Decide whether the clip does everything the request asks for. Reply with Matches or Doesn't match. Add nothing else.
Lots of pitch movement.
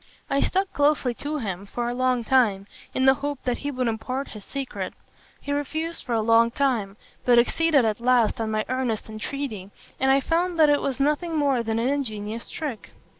Doesn't match